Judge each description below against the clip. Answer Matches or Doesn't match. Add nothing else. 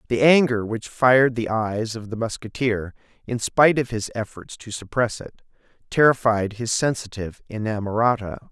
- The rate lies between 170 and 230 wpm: Doesn't match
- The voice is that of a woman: Doesn't match